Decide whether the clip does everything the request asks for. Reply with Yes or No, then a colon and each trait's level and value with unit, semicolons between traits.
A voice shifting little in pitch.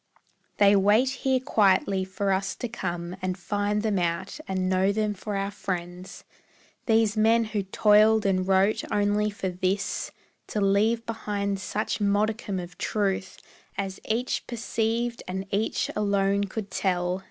Yes: narrow, 2.2 semitones